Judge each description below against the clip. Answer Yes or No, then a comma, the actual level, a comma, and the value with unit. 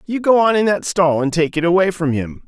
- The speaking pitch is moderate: Yes, medium, 175 Hz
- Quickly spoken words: Yes, fast, 290 wpm